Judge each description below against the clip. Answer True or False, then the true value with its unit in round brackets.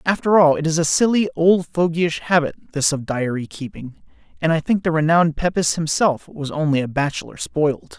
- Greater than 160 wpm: True (190 wpm)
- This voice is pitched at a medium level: True (160 Hz)